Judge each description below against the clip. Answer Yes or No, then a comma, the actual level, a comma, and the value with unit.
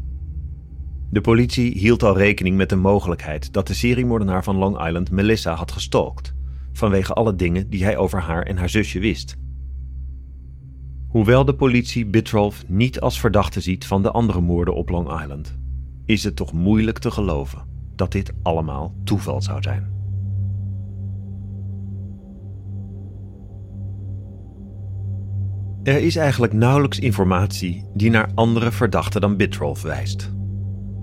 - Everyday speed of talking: No, slow, 130 wpm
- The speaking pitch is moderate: No, low, 100 Hz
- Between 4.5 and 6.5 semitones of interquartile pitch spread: No, average, 2.9 semitones